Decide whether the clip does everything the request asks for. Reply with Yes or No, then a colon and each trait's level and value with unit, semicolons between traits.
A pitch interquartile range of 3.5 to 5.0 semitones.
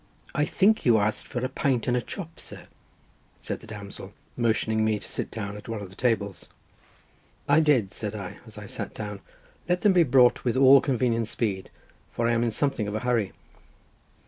Yes: average, 3.8 semitones